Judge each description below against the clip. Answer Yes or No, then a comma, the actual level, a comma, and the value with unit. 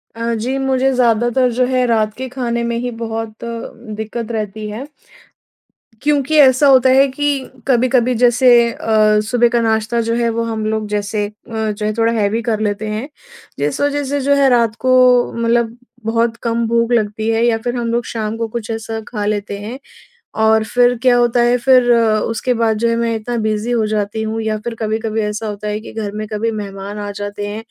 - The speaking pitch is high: Yes, high, 230 Hz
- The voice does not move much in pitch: Yes, narrow, 2.0 semitones